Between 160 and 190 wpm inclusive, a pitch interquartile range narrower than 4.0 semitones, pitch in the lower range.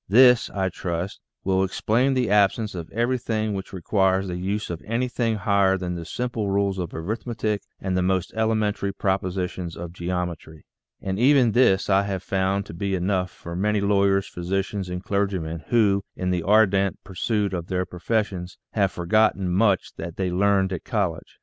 Yes: average, 175 wpm; narrow, 2.6 semitones; very low, 95 Hz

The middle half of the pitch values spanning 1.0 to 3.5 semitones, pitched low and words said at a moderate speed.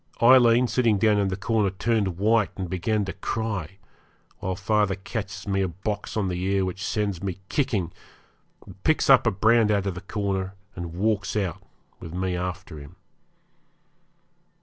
Yes: narrow, 2.5 semitones; low, 100 Hz; average, 165 wpm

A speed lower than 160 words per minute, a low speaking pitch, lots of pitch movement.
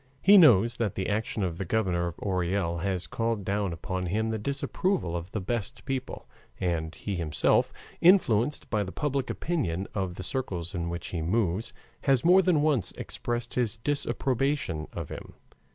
No: average, 170 wpm; low, 105 Hz; wide, 6.4 semitones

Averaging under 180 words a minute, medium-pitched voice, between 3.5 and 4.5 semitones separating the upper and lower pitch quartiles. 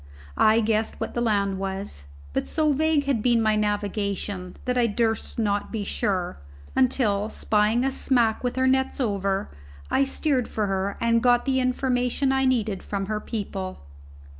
No: average, 165 wpm; high, 225 Hz; average, 3.9 semitones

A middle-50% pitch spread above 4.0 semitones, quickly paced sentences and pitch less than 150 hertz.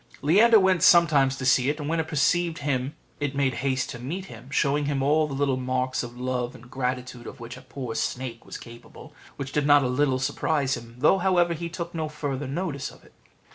No: average, 3.6 semitones; fast, 220 wpm; medium, 140 Hz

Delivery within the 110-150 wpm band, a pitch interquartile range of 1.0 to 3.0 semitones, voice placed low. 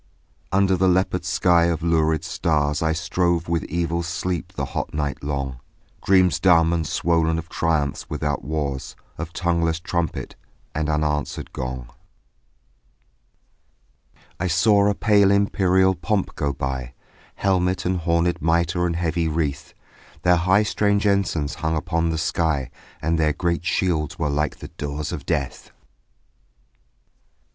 Yes: slow, 135 wpm; average, 2.7 semitones; very low, 85 Hz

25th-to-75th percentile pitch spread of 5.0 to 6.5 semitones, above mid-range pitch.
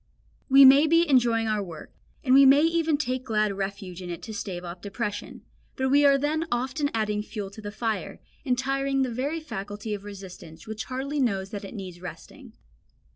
Yes: wide, 5.4 semitones; high, 225 Hz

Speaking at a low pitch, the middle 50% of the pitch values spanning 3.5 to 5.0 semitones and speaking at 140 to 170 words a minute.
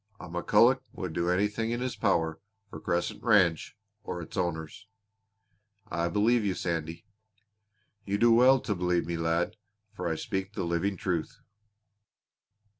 Yes: very low, 90 Hz; average, 3.8 semitones; average, 145 wpm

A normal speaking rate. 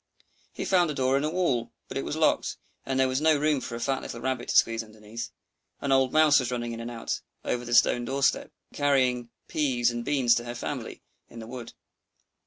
No: fast, 225 wpm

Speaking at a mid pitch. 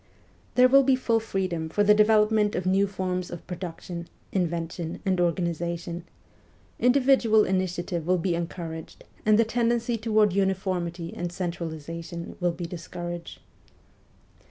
Yes: medium, 180 Hz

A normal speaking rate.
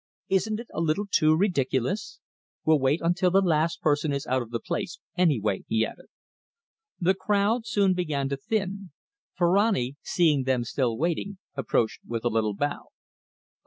Yes: average, 160 wpm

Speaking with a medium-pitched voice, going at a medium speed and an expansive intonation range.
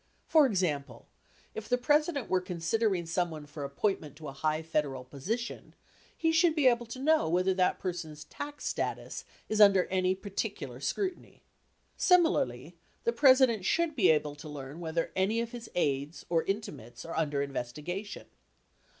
Yes: medium, 180 Hz; average, 155 wpm; wide, 7.6 semitones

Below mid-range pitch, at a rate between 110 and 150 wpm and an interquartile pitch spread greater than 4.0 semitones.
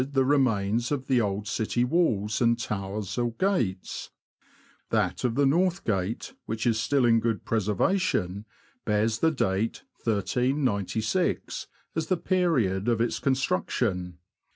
Yes: low, 115 Hz; slow, 135 wpm; average, 4.7 semitones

